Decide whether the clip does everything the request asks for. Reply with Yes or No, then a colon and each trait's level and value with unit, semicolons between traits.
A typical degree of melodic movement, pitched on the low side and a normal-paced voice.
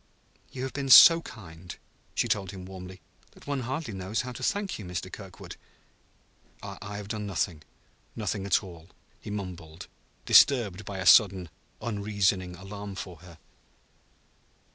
Yes: average, 3.3 semitones; low, 100 Hz; average, 145 wpm